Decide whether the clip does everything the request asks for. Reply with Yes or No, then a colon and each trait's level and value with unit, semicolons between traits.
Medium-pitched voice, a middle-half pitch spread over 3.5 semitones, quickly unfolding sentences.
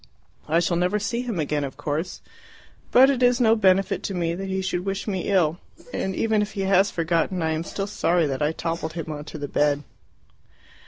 Yes: medium, 180 Hz; average, 3.9 semitones; fast, 215 wpm